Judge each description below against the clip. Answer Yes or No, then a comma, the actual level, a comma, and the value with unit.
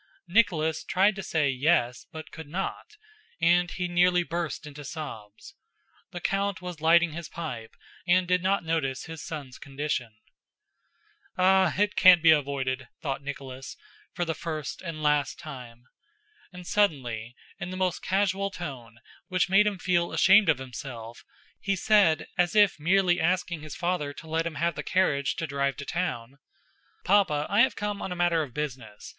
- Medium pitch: Yes, medium, 165 Hz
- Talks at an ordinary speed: Yes, average, 165 wpm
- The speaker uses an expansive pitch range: No, average, 4.6 semitones